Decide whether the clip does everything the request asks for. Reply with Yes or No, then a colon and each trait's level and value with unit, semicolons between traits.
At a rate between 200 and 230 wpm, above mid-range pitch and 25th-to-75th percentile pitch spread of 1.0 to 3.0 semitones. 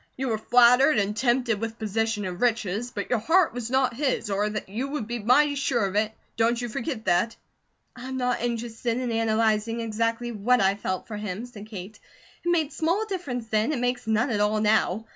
Yes: fast, 205 wpm; high, 230 Hz; narrow, 2.6 semitones